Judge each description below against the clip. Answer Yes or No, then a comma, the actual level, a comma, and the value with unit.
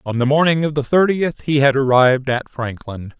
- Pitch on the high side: No, medium, 140 Hz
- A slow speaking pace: No, fast, 205 wpm